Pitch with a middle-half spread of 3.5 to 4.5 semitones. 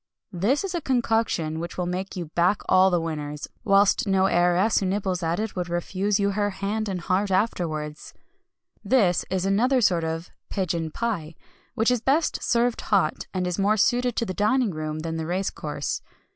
Yes: average, 4.1 semitones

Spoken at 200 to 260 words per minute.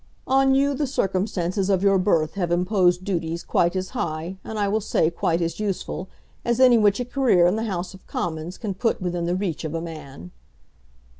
Yes: fast, 205 wpm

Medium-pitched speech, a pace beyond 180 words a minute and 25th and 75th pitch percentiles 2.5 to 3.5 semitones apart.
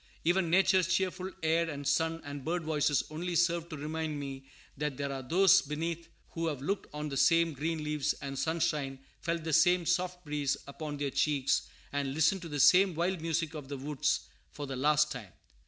Yes: medium, 155 Hz; average, 190 wpm; average, 2.8 semitones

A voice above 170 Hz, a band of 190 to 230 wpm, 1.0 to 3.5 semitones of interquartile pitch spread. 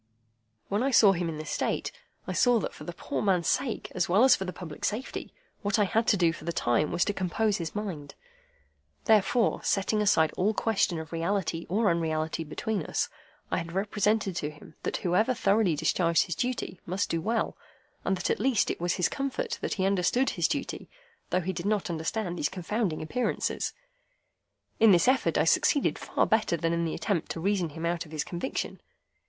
No: medium, 185 Hz; average, 200 wpm; average, 4.4 semitones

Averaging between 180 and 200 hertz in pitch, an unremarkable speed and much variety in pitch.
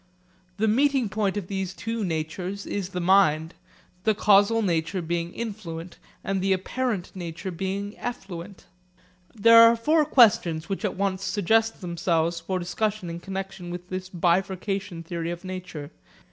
No: high, 190 Hz; average, 145 wpm; average, 3.3 semitones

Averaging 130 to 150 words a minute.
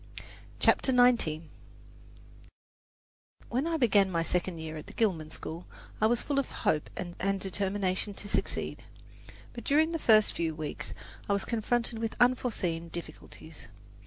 Yes: average, 140 wpm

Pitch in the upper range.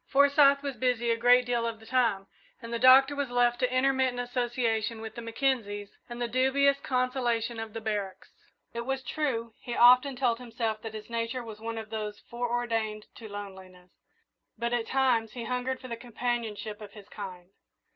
Yes: high, 235 Hz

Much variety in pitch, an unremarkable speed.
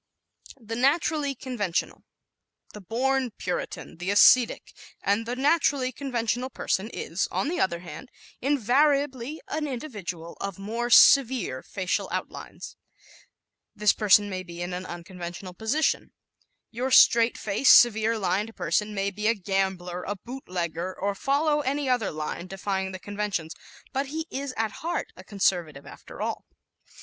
Yes: wide, 5.9 semitones; average, 145 wpm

